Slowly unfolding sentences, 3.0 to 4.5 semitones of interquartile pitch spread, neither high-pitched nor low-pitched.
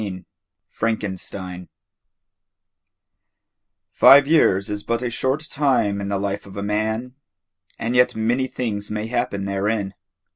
No: slow, 125 wpm; average, 3.7 semitones; low, 105 Hz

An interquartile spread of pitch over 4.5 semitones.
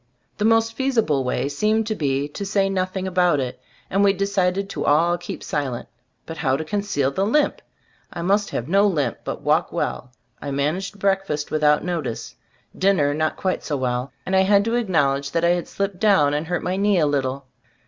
Yes: wide, 5.5 semitones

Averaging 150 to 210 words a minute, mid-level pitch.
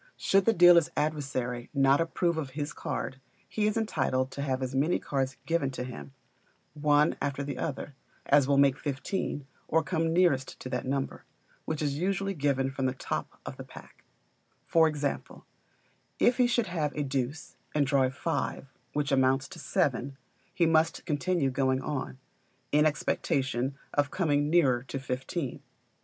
Yes: average, 165 wpm; medium, 145 Hz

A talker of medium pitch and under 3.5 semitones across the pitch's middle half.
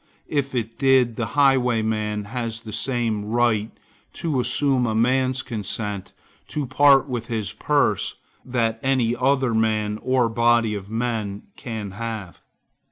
No: low, 115 Hz; average, 2.9 semitones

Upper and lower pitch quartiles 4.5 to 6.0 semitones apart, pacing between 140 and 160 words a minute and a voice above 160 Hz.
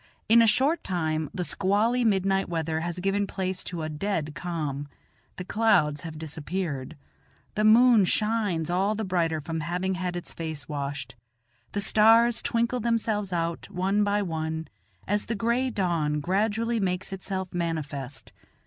Yes: average, 4.8 semitones; average, 150 wpm; medium, 185 Hz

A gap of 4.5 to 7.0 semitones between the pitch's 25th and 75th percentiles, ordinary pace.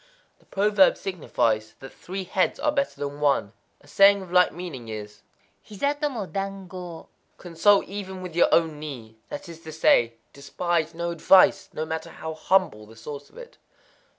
Yes: average, 5.1 semitones; average, 175 wpm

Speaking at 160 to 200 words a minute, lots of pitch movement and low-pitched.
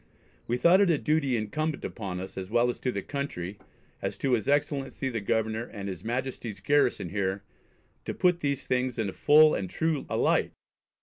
Yes: average, 190 wpm; wide, 6.0 semitones; low, 125 Hz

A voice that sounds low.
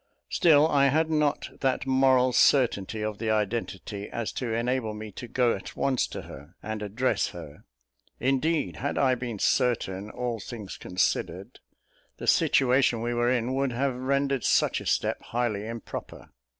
Yes: low, 125 Hz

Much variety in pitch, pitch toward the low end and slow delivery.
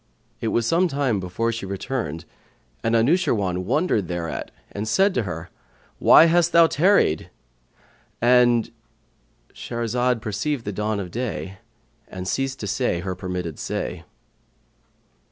Yes: wide, 6.0 semitones; low, 110 Hz; slow, 125 wpm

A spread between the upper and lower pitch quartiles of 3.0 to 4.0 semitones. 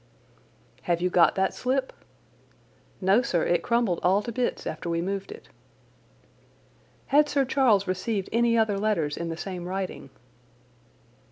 No: average, 5.0 semitones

